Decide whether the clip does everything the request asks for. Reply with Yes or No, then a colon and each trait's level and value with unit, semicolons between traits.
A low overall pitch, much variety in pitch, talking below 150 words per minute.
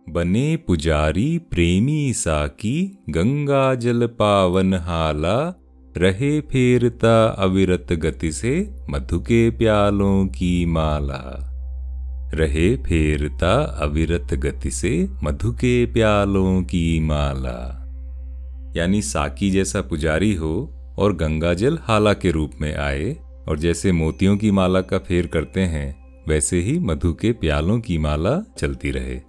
Yes: very low, 85 Hz; wide, 5.7 semitones; average, 115 wpm